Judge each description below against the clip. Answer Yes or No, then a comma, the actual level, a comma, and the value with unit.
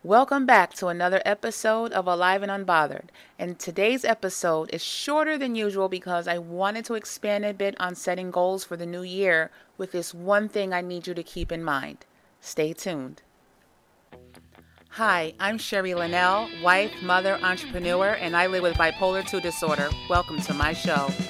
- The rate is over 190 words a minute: No, average, 170 wpm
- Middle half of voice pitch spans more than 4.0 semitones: No, narrow, 2.4 semitones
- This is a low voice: No, medium, 180 Hz